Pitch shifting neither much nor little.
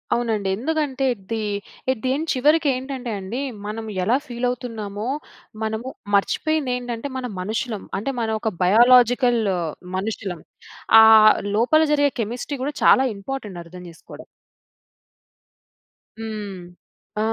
Yes: average, 3.3 semitones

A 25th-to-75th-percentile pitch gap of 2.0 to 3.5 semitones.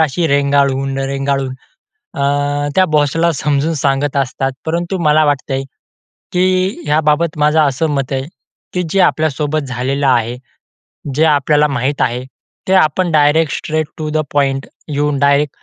Yes: narrow, 2.4 semitones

